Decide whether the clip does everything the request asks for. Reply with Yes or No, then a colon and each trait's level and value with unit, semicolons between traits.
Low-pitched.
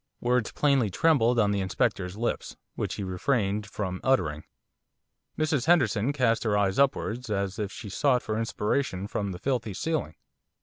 Yes: low, 110 Hz